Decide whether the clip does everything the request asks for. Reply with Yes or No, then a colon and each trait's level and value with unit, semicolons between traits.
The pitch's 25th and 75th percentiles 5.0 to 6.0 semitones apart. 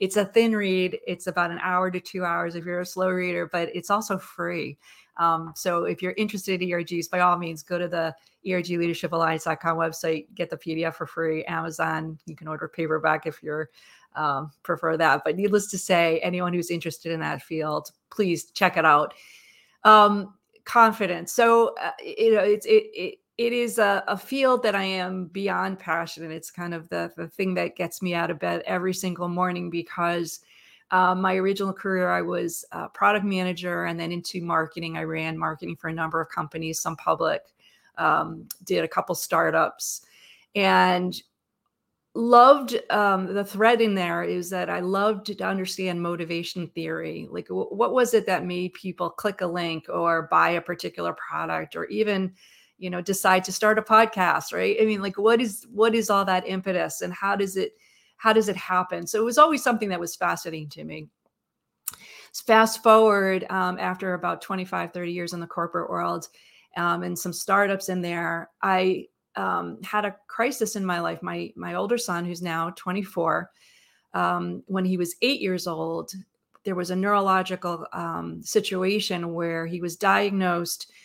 No: average, 3.0 semitones